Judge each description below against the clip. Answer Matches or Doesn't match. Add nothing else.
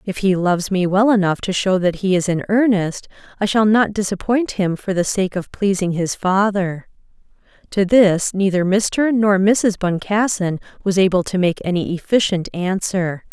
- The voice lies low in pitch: Doesn't match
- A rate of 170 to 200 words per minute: Matches